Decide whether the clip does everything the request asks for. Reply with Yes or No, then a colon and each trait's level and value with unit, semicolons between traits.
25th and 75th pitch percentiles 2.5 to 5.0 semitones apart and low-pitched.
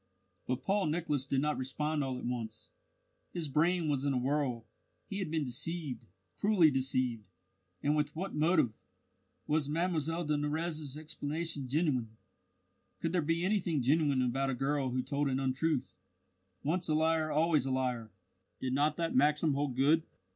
No: average, 3.6 semitones; medium, 150 Hz